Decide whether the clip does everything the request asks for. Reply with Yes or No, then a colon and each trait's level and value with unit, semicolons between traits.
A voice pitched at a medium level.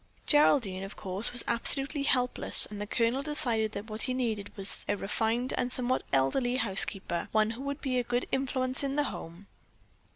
No: high, 235 Hz